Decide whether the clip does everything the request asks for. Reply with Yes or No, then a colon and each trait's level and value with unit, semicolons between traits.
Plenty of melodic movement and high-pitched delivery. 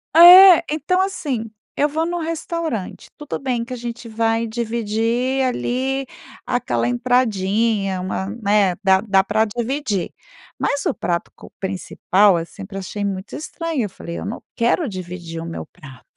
Yes: wide, 5.7 semitones; high, 225 Hz